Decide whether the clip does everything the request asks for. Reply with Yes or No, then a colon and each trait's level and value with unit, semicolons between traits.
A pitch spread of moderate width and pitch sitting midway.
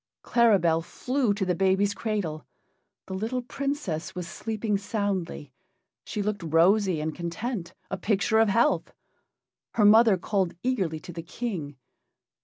No: average, 4.4 semitones; high, 195 Hz